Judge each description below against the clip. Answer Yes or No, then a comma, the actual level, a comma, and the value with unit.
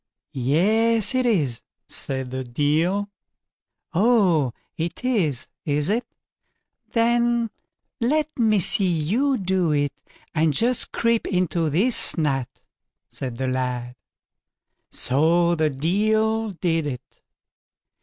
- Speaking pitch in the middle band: Yes, medium, 175 Hz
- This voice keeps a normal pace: No, slow, 105 wpm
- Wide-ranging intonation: Yes, wide, 7.5 semitones